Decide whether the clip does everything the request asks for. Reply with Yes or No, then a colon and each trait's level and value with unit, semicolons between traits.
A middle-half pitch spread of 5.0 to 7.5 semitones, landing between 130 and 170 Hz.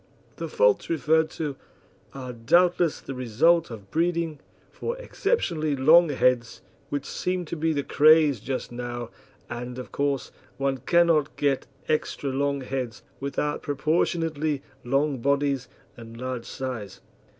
No: average, 4.0 semitones; medium, 140 Hz